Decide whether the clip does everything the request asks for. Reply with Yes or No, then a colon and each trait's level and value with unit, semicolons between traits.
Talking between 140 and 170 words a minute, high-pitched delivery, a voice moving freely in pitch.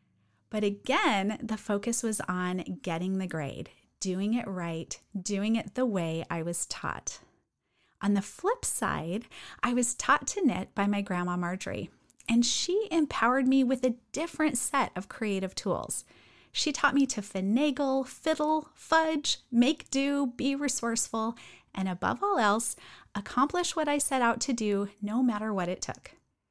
Yes: average, 160 wpm; high, 230 Hz; wide, 5.8 semitones